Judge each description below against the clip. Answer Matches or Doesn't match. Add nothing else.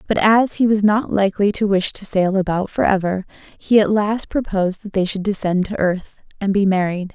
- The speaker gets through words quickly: Matches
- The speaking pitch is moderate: Doesn't match